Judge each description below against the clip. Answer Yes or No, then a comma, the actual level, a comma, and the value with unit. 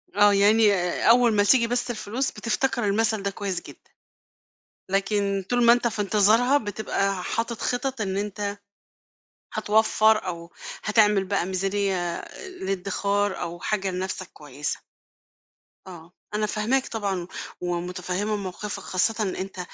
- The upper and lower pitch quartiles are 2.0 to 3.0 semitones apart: Yes, average, 2.7 semitones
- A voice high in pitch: Yes, high, 205 Hz